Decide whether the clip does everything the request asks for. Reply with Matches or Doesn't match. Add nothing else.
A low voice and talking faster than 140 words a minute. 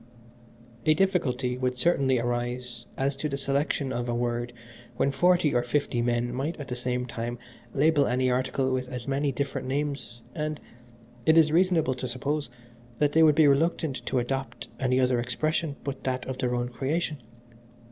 Matches